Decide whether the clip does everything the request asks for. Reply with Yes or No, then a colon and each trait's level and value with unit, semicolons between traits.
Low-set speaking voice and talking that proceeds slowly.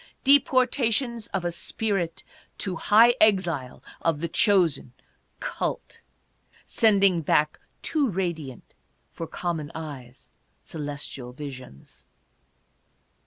No: medium, 170 Hz; slow, 95 wpm